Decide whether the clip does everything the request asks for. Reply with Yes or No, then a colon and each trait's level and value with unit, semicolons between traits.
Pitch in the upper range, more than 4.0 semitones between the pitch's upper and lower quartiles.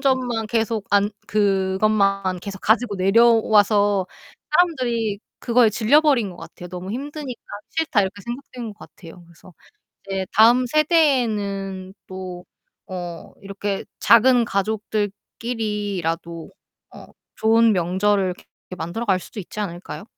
No: high, 210 Hz; average, 3.6 semitones